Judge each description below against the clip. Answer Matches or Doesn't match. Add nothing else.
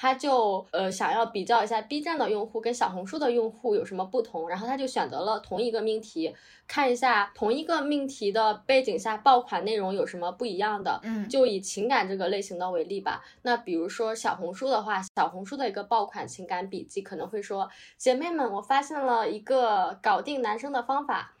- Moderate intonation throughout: Matches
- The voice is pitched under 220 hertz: Doesn't match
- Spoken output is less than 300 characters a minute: Doesn't match